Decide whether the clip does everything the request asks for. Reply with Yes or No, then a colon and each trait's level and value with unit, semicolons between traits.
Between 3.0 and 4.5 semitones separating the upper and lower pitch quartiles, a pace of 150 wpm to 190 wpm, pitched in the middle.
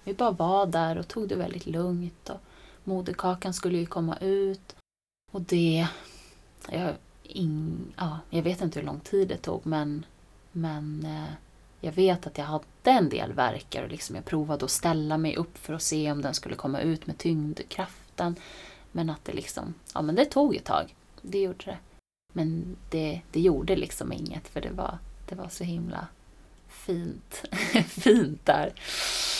Yes: average, 3.4 semitones; average, 175 wpm; medium, 170 Hz